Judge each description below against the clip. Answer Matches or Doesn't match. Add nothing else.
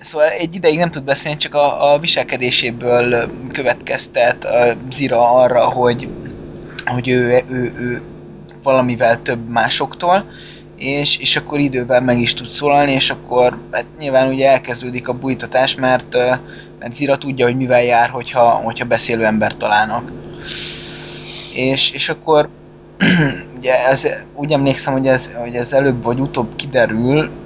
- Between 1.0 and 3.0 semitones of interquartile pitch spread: Matches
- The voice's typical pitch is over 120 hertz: Matches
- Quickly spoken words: Doesn't match